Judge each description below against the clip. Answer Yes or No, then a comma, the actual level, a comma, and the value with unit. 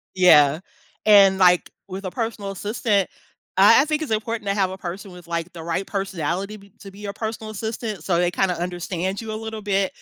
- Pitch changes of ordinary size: Yes, average, 3.0 semitones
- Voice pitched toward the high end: Yes, high, 195 Hz